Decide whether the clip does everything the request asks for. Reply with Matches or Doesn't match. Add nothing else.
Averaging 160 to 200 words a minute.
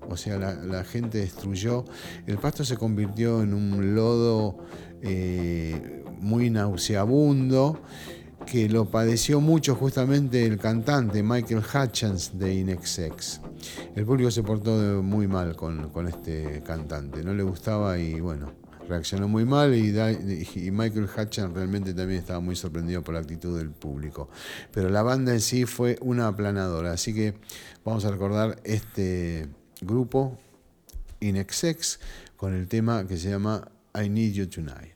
Doesn't match